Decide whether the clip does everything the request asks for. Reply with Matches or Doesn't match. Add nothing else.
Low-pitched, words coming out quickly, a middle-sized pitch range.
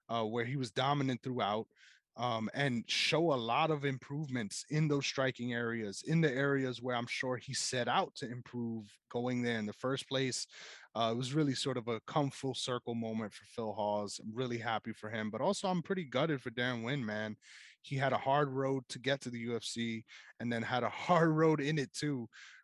Matches